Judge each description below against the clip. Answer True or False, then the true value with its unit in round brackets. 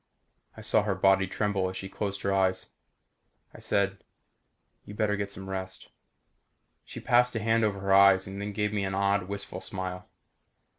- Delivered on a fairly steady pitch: True (1.3 semitones)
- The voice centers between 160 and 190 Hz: False (100 Hz)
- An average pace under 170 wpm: False (180 wpm)